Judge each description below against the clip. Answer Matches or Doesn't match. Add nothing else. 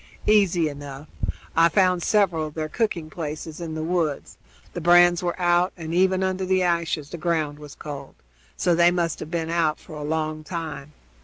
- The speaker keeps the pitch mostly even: Matches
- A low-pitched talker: Doesn't match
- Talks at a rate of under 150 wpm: Doesn't match